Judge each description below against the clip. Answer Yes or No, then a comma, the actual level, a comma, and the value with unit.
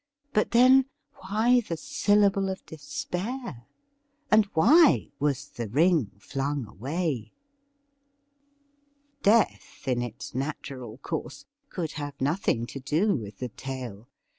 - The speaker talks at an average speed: No, slow, 115 wpm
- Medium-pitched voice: Yes, medium, 160 Hz